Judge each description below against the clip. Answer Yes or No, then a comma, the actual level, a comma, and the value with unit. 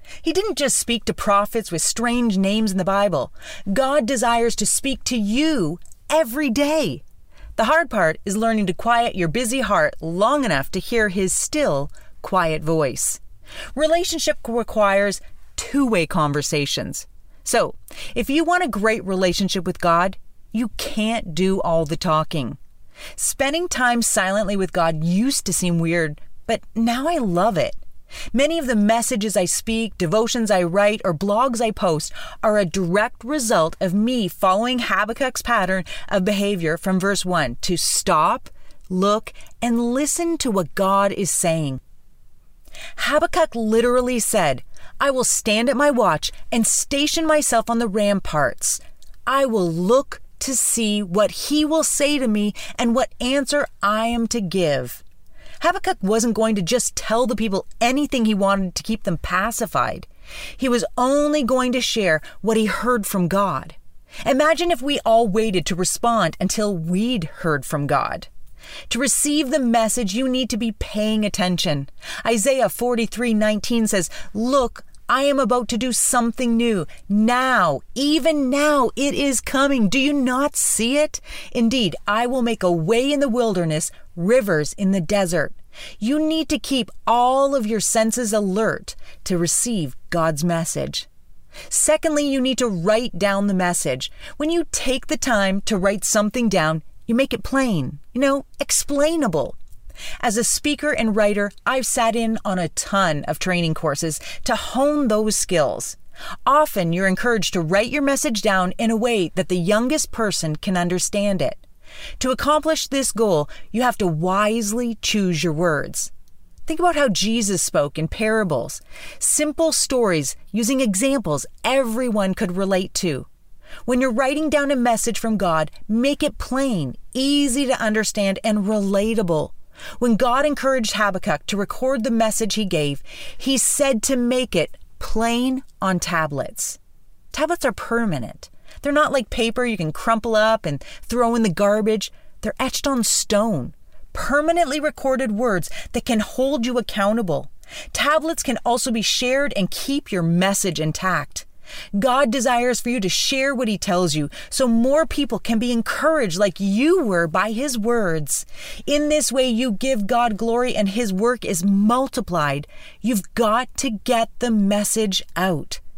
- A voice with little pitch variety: No, average, 5.2 semitones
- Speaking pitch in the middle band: No, high, 225 Hz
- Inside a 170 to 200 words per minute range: No, average, 160 wpm